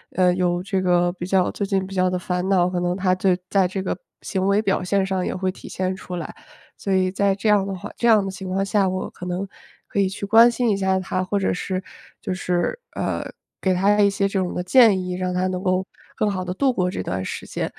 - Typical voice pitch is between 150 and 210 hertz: Yes, high, 190 Hz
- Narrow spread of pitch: Yes, narrow, 1.4 semitones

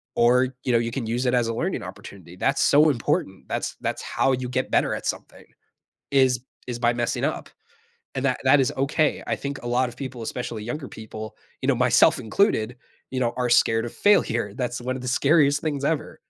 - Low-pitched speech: Yes, low, 125 Hz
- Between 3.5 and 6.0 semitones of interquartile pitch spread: No, narrow, 2.5 semitones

